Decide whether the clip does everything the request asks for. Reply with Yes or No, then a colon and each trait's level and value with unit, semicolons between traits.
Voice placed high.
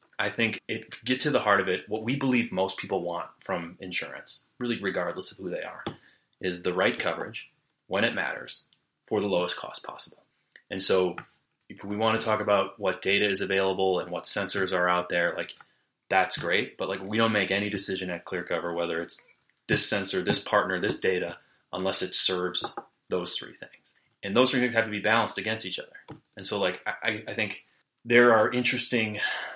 No: low, 100 Hz